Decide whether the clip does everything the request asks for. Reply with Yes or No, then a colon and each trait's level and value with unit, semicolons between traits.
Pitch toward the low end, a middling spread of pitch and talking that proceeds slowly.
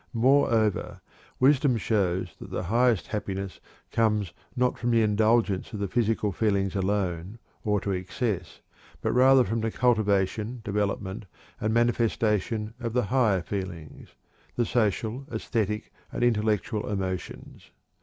Yes: low, 105 Hz; average, 3.1 semitones; slow, 125 wpm